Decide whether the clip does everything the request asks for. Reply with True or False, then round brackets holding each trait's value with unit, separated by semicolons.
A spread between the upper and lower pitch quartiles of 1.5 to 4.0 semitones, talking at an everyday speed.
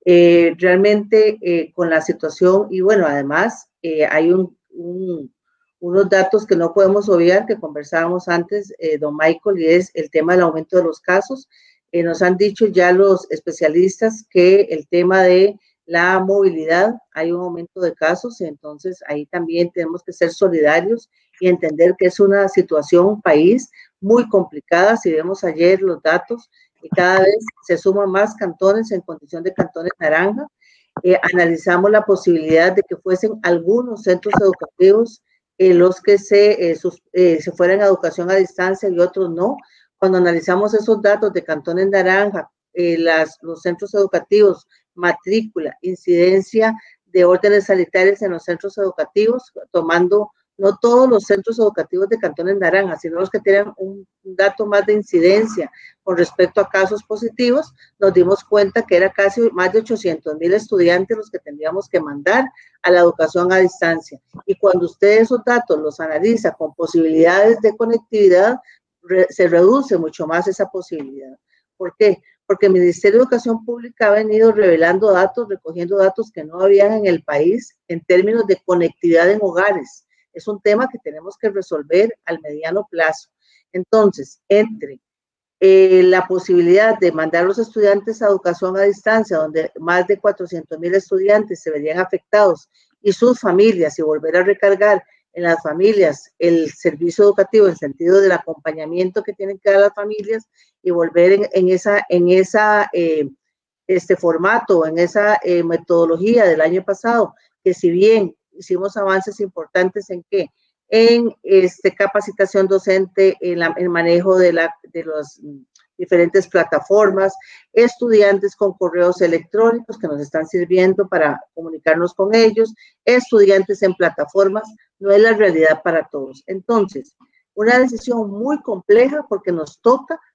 True (3.1 semitones; 155 wpm)